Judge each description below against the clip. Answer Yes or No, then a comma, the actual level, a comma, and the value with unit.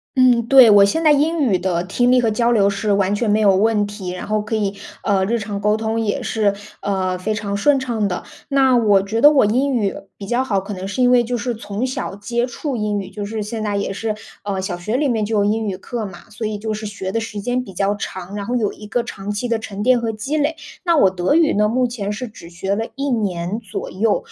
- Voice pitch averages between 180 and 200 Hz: No, high, 215 Hz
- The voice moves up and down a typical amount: Yes, average, 3.3 semitones